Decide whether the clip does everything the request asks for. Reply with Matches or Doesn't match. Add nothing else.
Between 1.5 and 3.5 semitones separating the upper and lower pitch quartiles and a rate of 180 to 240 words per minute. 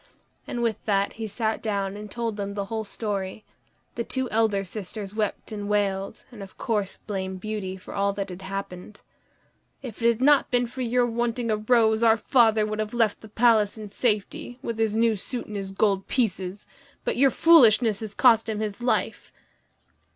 Matches